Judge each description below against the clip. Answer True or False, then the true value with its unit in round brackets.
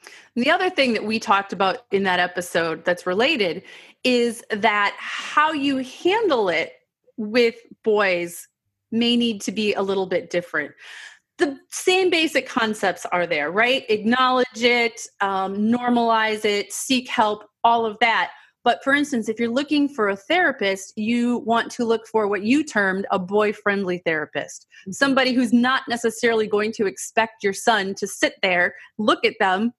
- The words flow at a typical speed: True (165 wpm)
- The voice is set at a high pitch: True (225 Hz)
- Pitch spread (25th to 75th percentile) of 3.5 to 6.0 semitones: True (4.3 semitones)